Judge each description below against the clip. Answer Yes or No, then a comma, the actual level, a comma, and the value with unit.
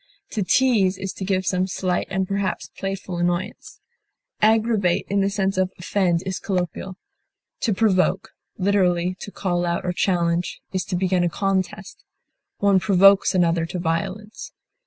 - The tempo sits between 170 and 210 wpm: No, average, 150 wpm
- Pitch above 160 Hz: Yes, high, 190 Hz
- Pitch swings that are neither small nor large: No, narrow, 1.8 semitones